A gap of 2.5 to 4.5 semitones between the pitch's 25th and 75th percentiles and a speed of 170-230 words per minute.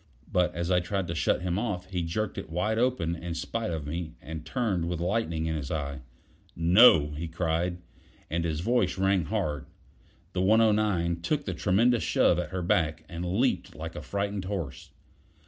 Yes: average, 3.7 semitones; average, 180 wpm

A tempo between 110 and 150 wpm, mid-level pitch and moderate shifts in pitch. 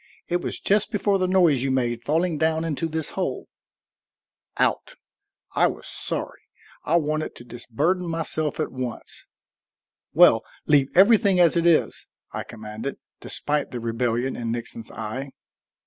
No: average, 145 wpm; medium, 150 Hz; wide, 5.8 semitones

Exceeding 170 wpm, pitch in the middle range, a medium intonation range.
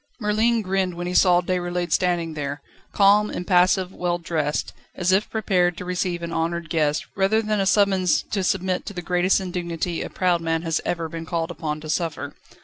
No: average, 190 wpm; medium, 180 Hz; narrow, 2.2 semitones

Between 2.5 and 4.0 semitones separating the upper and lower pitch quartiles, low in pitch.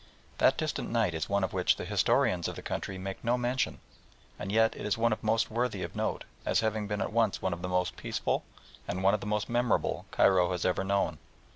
Yes: average, 3.3 semitones; low, 100 Hz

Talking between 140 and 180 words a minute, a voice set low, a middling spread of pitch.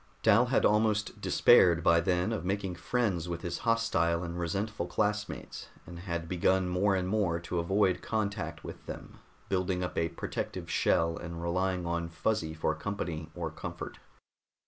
Yes: average, 160 wpm; very low, 90 Hz; average, 3.2 semitones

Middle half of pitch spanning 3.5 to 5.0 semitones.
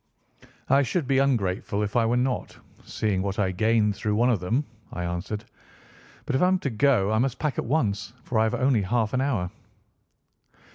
Yes: average, 4.7 semitones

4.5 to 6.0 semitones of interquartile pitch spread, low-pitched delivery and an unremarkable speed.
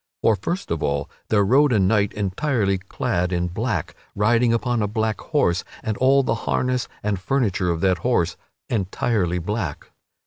Yes: average, 4.9 semitones; low, 105 Hz; average, 170 wpm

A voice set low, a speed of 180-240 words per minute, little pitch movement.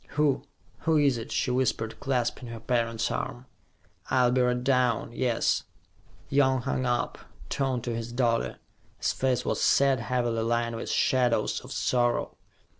No: low, 125 Hz; average, 150 wpm; narrow, 1.9 semitones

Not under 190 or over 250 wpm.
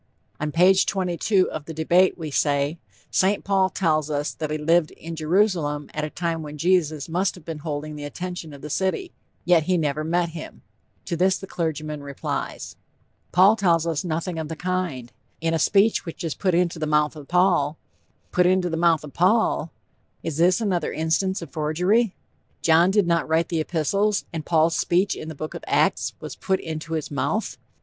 Yes: average, 195 wpm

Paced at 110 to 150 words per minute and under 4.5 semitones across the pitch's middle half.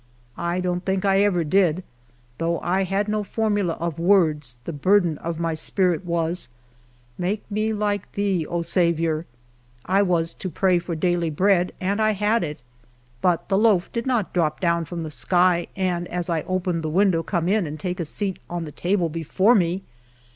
No: average, 190 wpm; average, 2.8 semitones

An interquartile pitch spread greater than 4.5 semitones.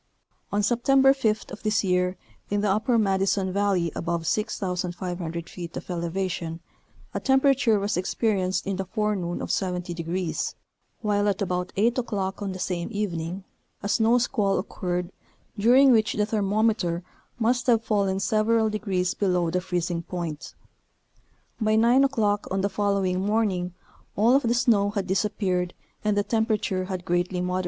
No: average, 3.1 semitones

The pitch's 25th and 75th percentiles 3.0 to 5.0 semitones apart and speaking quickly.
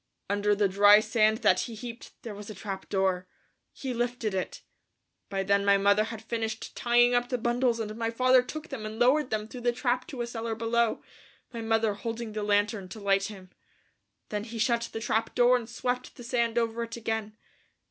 No: narrow, 2.5 semitones; fast, 210 wpm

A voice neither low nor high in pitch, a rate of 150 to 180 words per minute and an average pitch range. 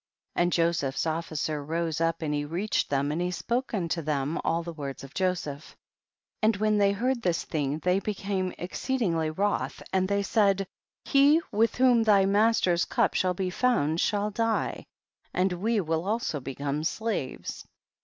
Yes: medium, 180 Hz; average, 165 wpm; average, 4.8 semitones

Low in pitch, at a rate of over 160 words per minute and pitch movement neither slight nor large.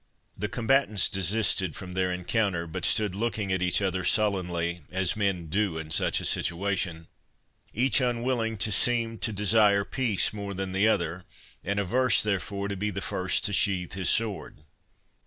Yes: low, 100 Hz; average, 170 wpm; average, 3.0 semitones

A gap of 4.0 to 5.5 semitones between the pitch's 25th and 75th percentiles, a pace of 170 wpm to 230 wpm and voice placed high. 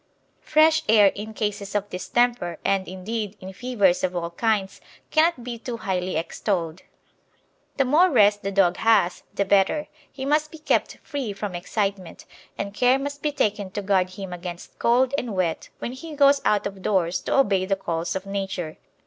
Yes: average, 4.8 semitones; average, 180 wpm; high, 200 Hz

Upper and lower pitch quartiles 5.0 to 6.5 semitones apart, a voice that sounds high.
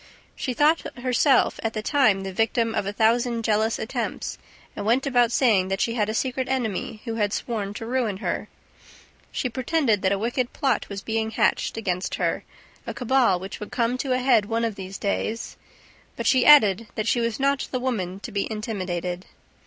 No: average, 3.6 semitones; high, 225 Hz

